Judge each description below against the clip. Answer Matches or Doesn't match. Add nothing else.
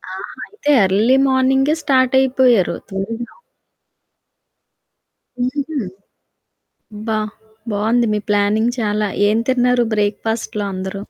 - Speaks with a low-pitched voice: Doesn't match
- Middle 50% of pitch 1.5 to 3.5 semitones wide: Doesn't match